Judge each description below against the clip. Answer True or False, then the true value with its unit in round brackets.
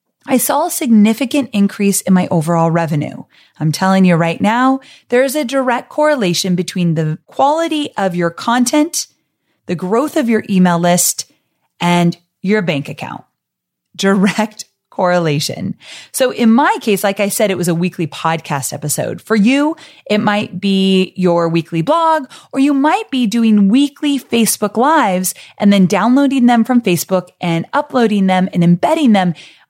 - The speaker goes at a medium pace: True (155 wpm)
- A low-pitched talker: False (200 Hz)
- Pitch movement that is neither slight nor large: False (6.4 semitones)